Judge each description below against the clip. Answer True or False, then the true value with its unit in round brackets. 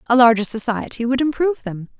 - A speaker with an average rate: True (180 wpm)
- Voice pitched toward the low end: False (245 Hz)